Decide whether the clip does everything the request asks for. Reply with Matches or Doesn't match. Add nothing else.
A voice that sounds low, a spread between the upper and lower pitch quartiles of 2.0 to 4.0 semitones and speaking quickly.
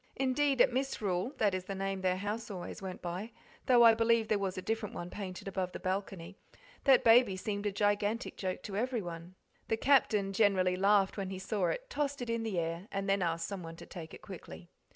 Doesn't match